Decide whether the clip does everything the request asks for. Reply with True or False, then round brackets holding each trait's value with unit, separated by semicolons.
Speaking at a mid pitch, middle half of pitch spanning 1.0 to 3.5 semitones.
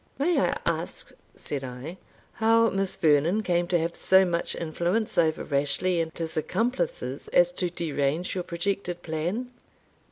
False (175 Hz; 4.7 semitones)